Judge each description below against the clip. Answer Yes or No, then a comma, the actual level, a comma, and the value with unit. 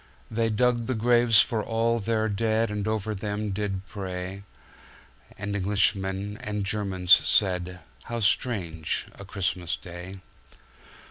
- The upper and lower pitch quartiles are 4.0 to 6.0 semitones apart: No, narrow, 2.6 semitones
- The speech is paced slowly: Yes, slow, 110 wpm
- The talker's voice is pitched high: No, low, 105 Hz